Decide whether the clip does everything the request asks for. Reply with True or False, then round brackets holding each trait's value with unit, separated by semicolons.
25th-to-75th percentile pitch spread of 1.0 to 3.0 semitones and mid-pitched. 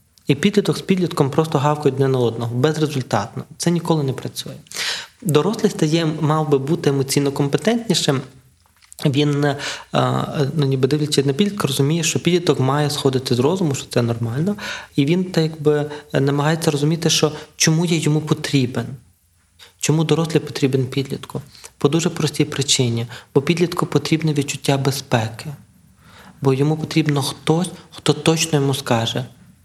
True (2.7 semitones; 145 Hz)